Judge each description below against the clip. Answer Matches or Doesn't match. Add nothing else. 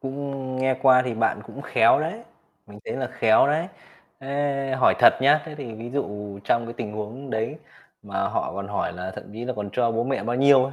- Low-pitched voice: Matches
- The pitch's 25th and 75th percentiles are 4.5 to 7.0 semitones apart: Doesn't match